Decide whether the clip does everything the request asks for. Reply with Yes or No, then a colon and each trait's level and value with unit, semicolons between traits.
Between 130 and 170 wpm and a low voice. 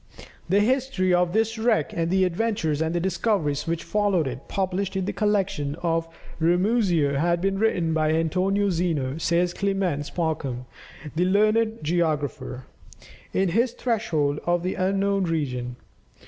No: average, 140 wpm; medium, 175 Hz